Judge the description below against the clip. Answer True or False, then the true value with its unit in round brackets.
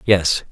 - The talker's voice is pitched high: False (95 Hz)